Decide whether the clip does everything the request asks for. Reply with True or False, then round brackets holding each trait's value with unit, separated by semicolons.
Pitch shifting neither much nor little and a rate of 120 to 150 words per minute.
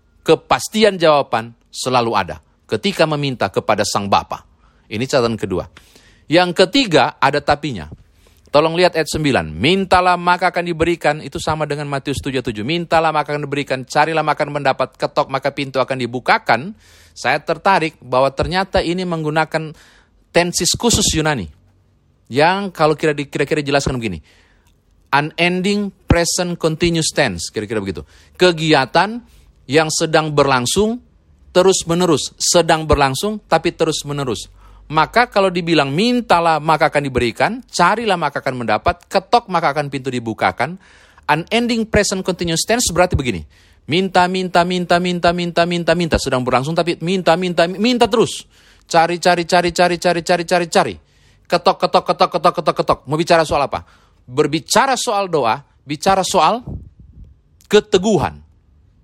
True (4.9 semitones; 135 wpm)